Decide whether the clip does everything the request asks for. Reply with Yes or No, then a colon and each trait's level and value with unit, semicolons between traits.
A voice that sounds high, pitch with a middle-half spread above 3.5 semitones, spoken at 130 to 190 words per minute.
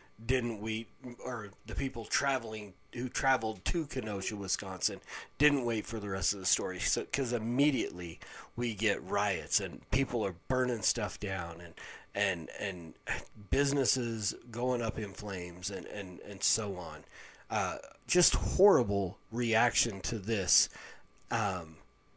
No: low, 110 Hz; average, 4.2 semitones; average, 140 wpm